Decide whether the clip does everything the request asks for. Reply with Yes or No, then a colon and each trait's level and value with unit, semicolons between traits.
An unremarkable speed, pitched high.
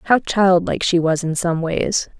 No: average, 190 wpm; medium, 180 Hz